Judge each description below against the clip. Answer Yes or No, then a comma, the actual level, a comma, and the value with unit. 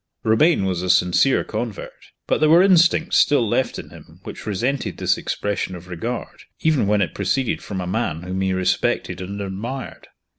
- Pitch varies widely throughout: Yes, wide, 6.4 semitones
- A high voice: No, low, 105 Hz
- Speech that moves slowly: No, average, 180 wpm